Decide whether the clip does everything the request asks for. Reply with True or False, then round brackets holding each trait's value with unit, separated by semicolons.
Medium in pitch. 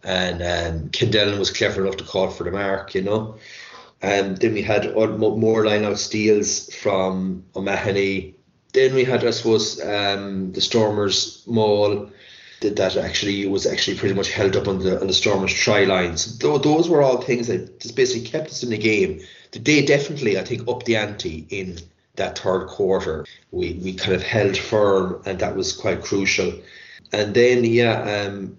False (105 Hz)